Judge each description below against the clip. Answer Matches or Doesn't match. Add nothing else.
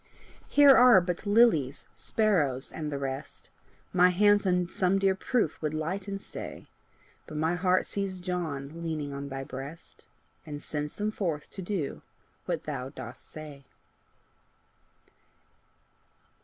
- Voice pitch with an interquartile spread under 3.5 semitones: Doesn't match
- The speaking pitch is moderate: Matches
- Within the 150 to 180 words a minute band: Doesn't match